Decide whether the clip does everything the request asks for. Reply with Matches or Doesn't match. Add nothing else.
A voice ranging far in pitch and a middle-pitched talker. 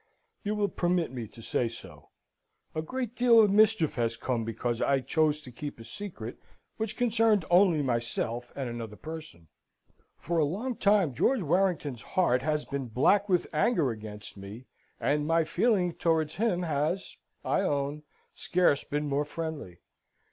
Matches